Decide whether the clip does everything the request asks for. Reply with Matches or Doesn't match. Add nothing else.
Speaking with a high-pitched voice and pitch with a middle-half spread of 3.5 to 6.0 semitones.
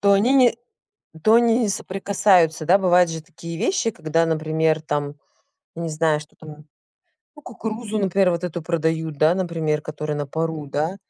Doesn't match